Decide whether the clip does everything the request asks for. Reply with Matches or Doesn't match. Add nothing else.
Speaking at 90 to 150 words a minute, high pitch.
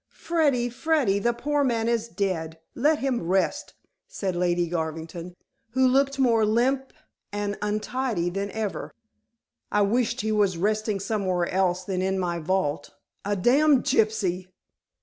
Matches